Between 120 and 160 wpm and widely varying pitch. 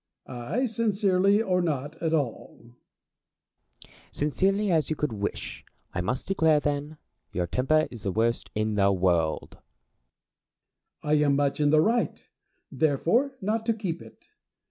Yes: average, 145 wpm; wide, 8.3 semitones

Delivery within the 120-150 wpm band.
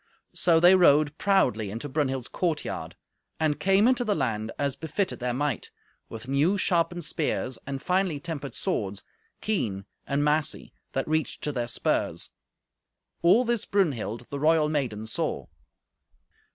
Yes: average, 140 wpm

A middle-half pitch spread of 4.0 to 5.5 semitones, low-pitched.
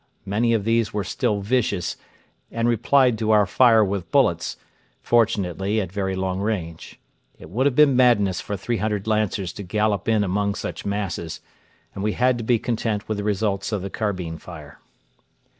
No: average, 2.9 semitones; low, 105 Hz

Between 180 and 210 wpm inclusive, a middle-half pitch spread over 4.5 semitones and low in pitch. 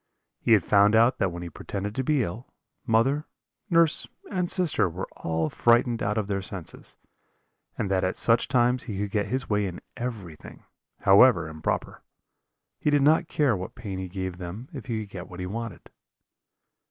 Yes: average, 185 wpm; average, 5.0 semitones; low, 105 Hz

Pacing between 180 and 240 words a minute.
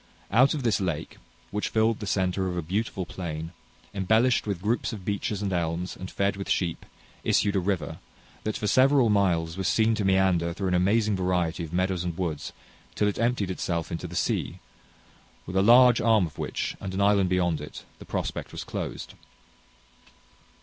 Yes: average, 185 wpm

